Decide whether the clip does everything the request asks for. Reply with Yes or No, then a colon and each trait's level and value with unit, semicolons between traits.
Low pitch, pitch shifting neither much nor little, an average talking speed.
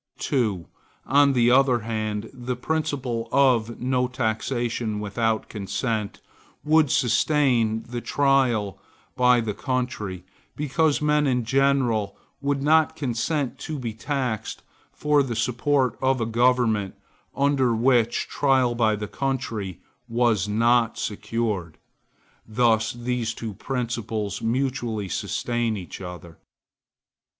No: low, 120 Hz; average, 3.4 semitones; slow, 115 wpm